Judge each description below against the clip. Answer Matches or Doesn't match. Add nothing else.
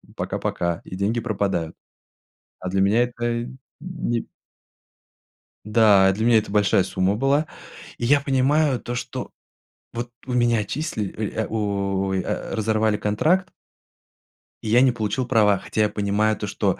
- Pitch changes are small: Doesn't match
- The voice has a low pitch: Matches